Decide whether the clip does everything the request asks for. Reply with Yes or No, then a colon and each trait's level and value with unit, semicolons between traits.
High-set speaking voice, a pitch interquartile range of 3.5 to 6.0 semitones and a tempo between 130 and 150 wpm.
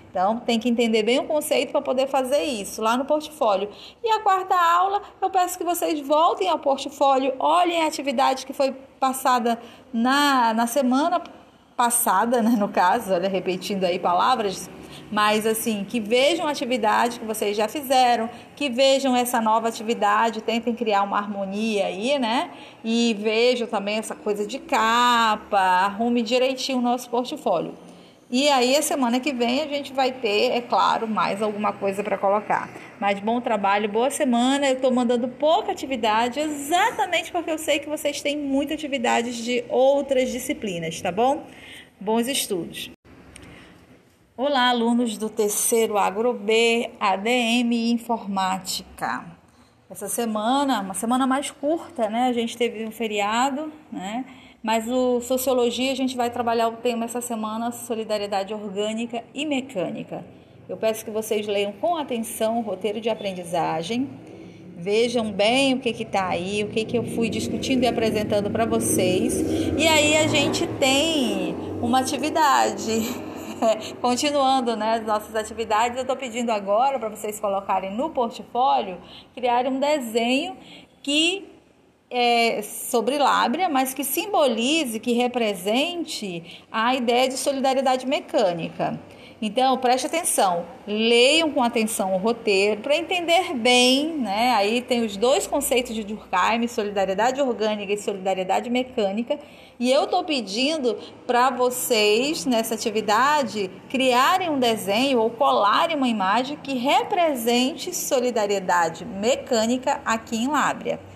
Yes: high, 245 Hz; average, 3.8 semitones; average, 145 wpm